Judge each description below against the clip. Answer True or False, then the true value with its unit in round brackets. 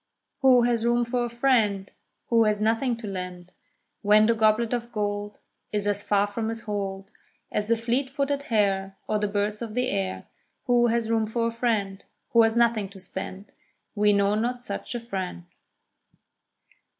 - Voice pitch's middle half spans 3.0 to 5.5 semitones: False (2.6 semitones)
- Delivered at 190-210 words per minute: False (175 wpm)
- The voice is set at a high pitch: True (220 Hz)